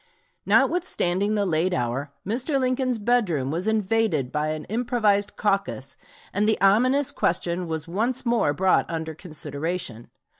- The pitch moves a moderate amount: No, wide, 6.1 semitones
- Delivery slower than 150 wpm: Yes, slow, 135 wpm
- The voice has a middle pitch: No, high, 195 Hz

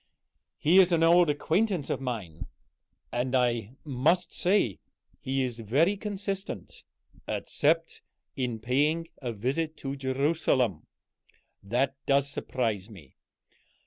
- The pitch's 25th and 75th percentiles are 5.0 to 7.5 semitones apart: Yes, wide, 5.4 semitones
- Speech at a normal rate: No, slow, 110 wpm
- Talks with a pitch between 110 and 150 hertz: Yes, low, 135 Hz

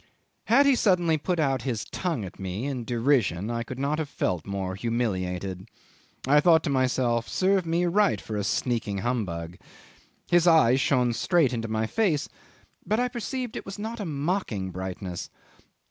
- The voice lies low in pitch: Yes, low, 130 Hz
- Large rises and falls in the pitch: Yes, wide, 8.7 semitones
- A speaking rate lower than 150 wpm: No, average, 170 wpm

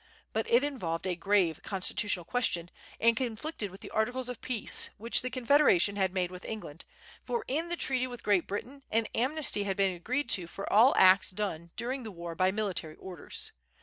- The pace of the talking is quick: No, average, 190 wpm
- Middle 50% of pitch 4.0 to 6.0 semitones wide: Yes, average, 5.3 semitones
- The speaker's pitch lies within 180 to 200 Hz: No, high, 210 Hz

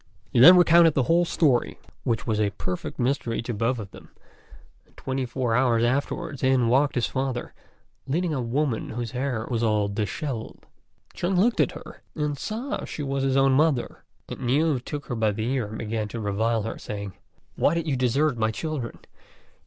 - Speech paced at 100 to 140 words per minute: No, average, 190 wpm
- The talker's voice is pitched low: Yes, low, 125 Hz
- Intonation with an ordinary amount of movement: Yes, average, 4.3 semitones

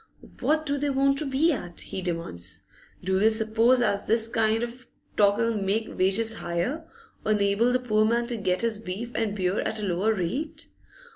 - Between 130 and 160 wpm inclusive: No, average, 195 wpm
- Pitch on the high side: Yes, high, 220 Hz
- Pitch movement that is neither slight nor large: Yes, average, 3.7 semitones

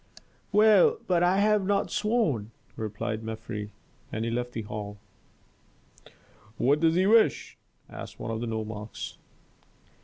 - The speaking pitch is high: No, low, 120 Hz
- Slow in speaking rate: Yes, slow, 130 wpm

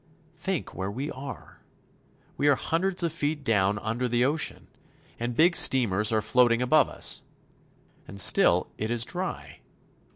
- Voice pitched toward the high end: No, low, 125 Hz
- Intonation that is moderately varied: No, wide, 5.8 semitones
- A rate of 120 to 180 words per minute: Yes, average, 150 wpm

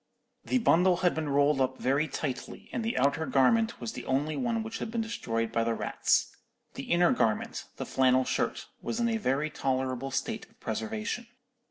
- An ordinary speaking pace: Yes, average, 180 wpm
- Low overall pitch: No, medium, 155 Hz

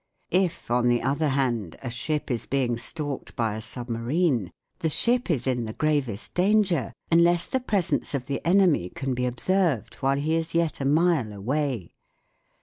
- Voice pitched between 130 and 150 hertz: Yes, medium, 140 Hz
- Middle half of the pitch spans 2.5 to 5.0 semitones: No, wide, 5.6 semitones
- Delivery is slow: No, average, 170 wpm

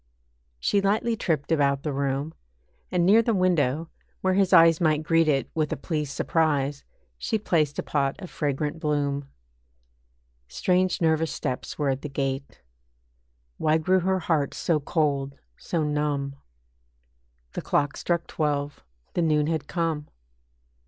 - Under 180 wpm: Yes, average, 145 wpm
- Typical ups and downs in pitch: Yes, average, 3.1 semitones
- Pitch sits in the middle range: Yes, medium, 155 Hz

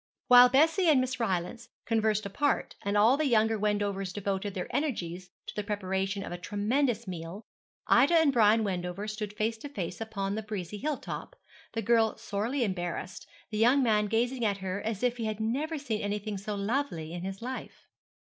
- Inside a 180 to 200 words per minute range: Yes, average, 190 wpm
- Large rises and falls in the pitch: No, average, 3.7 semitones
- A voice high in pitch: Yes, high, 215 Hz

